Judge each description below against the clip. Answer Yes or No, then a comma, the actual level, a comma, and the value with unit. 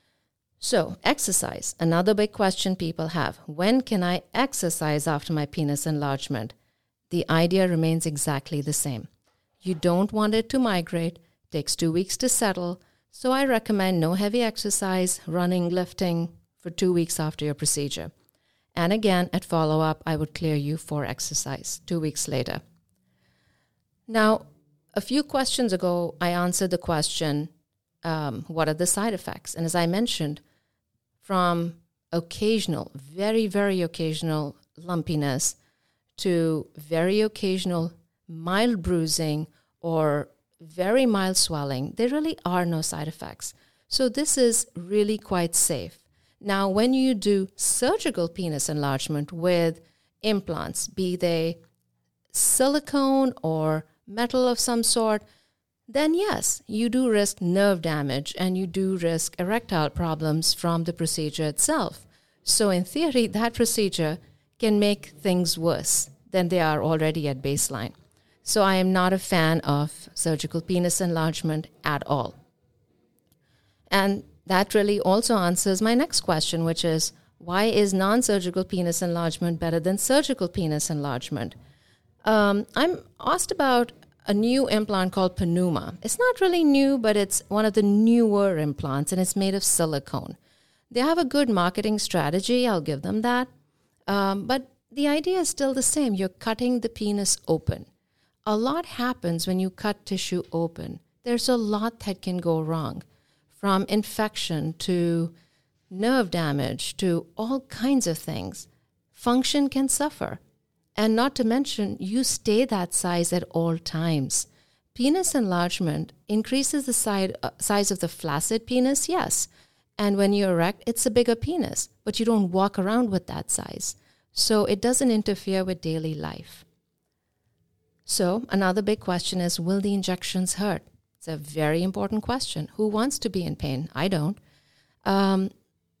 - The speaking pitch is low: No, medium, 180 Hz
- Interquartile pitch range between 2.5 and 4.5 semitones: No, average, 5.2 semitones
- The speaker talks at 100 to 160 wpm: Yes, average, 145 wpm